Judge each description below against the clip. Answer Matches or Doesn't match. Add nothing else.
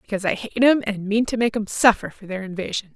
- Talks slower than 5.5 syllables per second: Doesn't match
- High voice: Matches